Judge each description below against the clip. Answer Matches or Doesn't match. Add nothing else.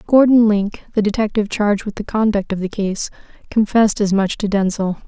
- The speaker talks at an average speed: Matches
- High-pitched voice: Matches